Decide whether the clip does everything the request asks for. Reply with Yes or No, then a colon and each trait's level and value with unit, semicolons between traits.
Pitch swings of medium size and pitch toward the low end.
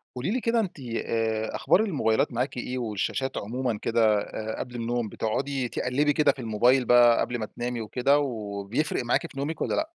Yes: average, 3.5 semitones; low, 120 Hz